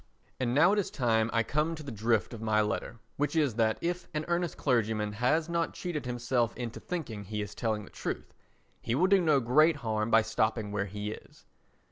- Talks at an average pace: No, fast, 210 wpm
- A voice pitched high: No, low, 120 Hz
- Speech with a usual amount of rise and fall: No, wide, 5.9 semitones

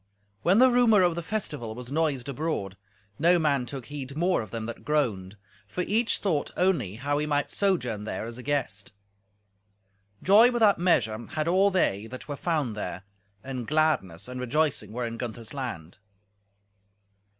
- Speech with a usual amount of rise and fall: No, wide, 6.8 semitones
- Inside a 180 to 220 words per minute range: No, average, 165 wpm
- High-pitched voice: No, medium, 145 Hz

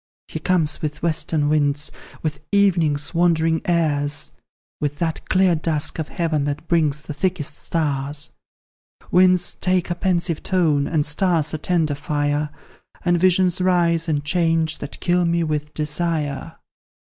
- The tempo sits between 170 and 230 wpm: No, average, 140 wpm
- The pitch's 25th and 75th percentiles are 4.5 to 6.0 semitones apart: No, average, 2.8 semitones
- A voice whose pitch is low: No, medium, 160 Hz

